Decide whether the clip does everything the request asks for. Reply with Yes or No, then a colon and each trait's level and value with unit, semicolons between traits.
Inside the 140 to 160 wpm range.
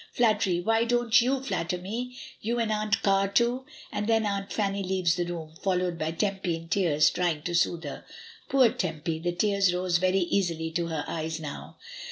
No: average, 190 wpm